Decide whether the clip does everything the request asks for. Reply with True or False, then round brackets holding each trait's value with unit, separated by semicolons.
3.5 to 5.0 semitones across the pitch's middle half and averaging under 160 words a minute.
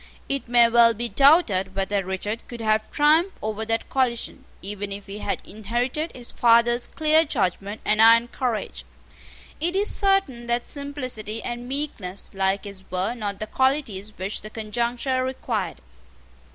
True (4.0 semitones; 150 wpm)